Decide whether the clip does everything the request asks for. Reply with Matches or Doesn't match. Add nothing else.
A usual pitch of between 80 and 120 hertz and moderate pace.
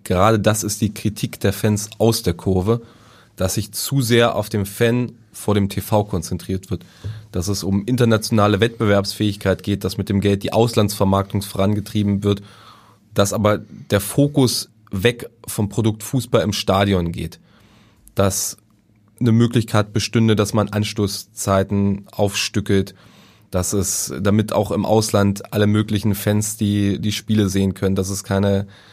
Matches